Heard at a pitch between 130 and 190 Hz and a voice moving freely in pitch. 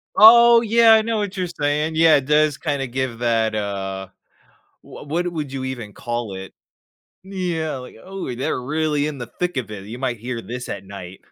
Yes: low, 135 Hz; wide, 6.6 semitones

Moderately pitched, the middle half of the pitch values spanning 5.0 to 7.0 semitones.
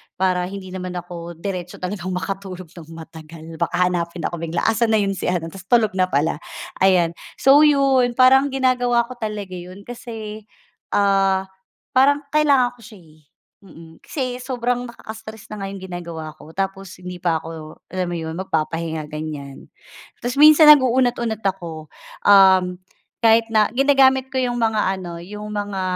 No: high, 195 Hz; wide, 5.5 semitones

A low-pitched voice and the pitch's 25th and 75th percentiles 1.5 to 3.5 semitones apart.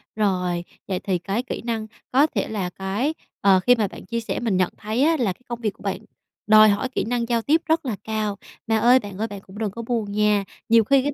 No: high, 215 Hz; average, 3.2 semitones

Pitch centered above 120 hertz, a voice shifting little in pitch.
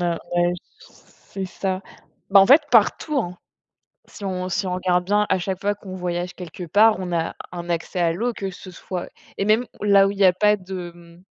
Yes: medium, 185 Hz; narrow, 2.2 semitones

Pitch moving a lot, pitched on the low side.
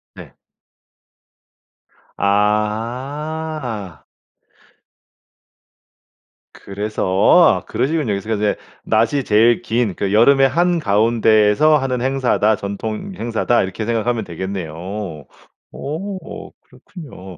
No: average, 4.8 semitones; low, 115 Hz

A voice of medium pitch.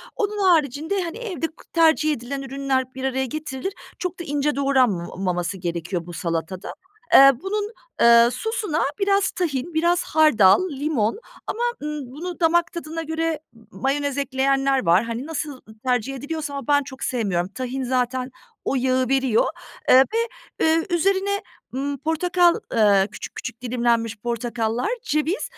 No: very high, 275 Hz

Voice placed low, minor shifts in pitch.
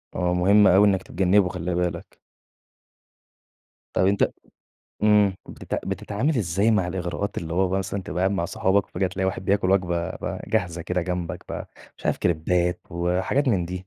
Yes: very low, 95 Hz; narrow, 2.0 semitones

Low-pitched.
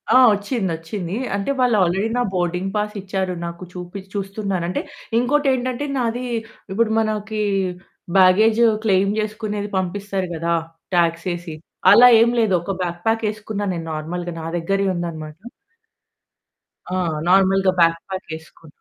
No: high, 195 Hz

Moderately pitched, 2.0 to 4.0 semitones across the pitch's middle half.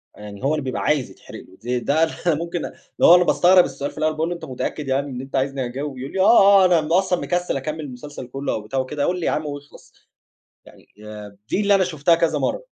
No: medium, 150 Hz; average, 4.7 semitones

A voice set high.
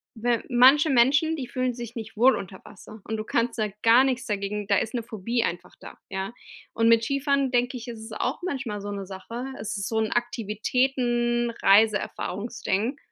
Yes: high, 230 Hz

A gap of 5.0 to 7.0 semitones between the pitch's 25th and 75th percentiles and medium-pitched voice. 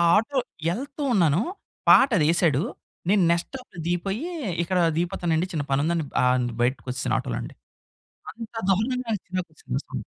Yes: wide, 5.6 semitones; medium, 175 Hz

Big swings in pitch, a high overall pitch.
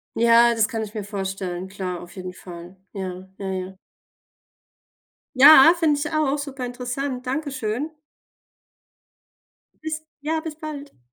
Yes: wide, 7.0 semitones; high, 235 Hz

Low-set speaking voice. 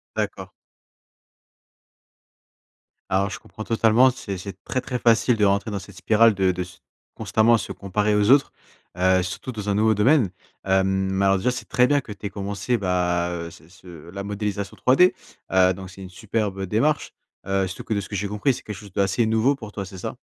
Yes: low, 100 Hz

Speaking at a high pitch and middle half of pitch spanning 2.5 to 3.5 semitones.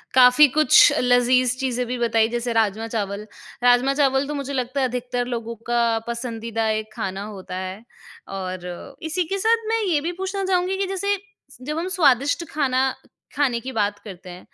No: very high, 250 Hz; average, 4.3 semitones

